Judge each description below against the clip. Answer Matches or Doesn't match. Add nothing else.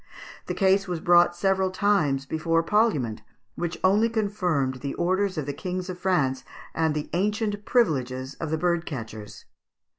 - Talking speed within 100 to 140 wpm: Doesn't match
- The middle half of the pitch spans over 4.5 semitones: Matches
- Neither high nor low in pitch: Matches